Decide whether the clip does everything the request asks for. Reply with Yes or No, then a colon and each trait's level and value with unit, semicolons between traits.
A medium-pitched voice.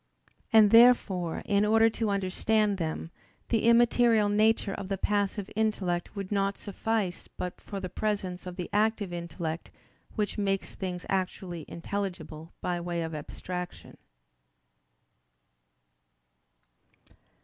No: high, 195 Hz